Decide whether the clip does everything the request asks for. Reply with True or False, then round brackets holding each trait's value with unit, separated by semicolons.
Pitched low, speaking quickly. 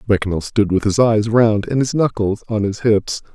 True (105 Hz; 215 wpm)